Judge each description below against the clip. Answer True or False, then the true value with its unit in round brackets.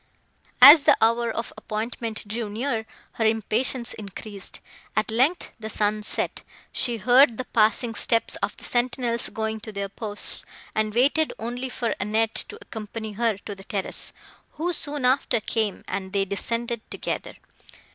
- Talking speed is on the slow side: False (155 wpm)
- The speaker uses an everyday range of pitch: False (2.3 semitones)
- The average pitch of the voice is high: True (225 Hz)